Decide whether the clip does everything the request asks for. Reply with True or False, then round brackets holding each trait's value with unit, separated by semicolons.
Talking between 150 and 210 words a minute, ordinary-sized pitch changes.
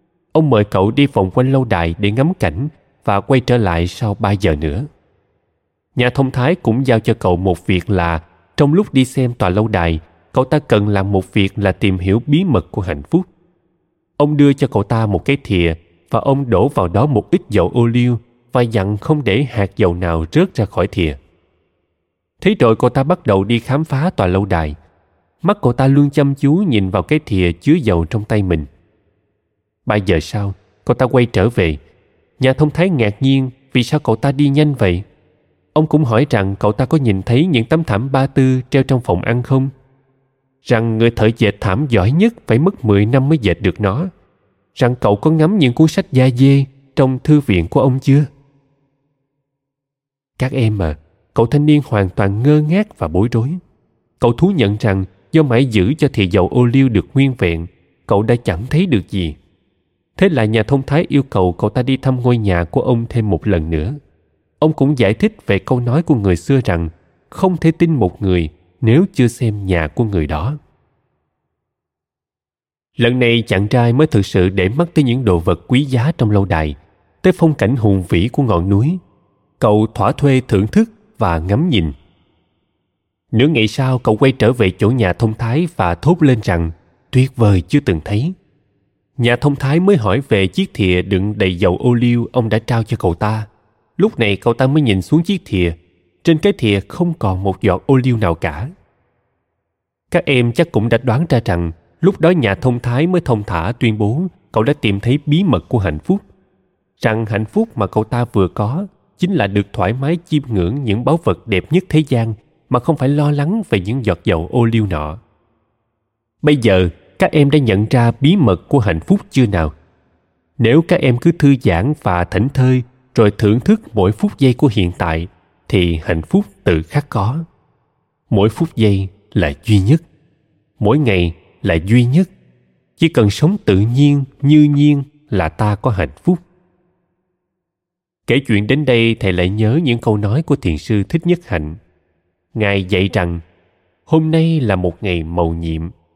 False (200 wpm; 6.6 semitones)